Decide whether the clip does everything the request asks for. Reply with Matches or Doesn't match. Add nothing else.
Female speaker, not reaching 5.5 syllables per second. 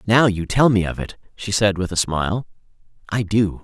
Doesn't match